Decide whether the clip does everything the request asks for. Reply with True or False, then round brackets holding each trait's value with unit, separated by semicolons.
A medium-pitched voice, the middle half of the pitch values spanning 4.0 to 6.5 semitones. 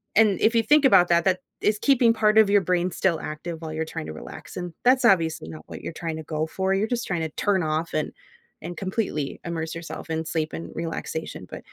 True (170 Hz; 4.3 semitones)